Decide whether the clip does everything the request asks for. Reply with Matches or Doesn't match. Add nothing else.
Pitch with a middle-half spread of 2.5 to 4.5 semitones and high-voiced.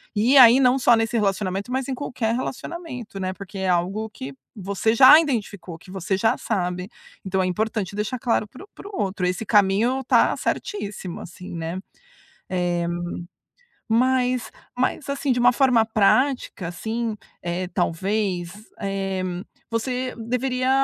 Doesn't match